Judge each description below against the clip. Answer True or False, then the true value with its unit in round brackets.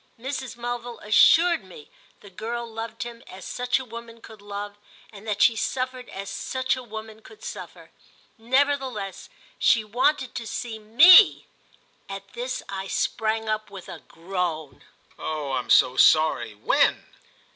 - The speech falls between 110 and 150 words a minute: True (145 wpm)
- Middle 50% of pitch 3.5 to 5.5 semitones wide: True (3.9 semitones)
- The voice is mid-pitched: False (225 Hz)